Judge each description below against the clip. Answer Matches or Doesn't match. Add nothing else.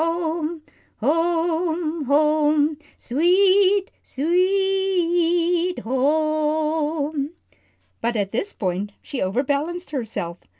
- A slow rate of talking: Matches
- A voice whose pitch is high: Matches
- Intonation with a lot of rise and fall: Doesn't match